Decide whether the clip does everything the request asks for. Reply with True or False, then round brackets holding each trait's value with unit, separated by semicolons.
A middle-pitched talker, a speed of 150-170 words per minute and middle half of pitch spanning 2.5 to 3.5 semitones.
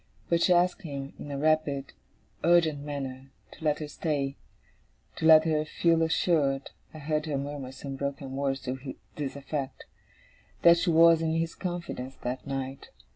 True (145 Hz; 165 wpm; 2.9 semitones)